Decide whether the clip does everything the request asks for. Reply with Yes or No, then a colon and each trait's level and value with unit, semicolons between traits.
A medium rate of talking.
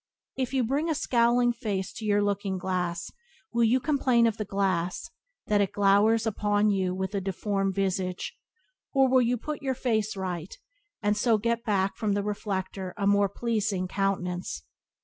Yes: average, 170 wpm